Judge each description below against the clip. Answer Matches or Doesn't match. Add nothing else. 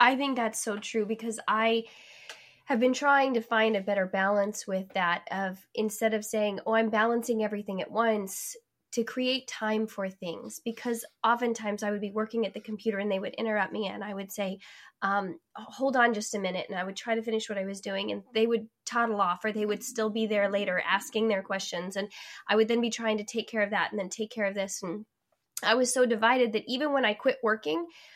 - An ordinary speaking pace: Doesn't match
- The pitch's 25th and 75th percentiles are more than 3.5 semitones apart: Doesn't match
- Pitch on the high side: Matches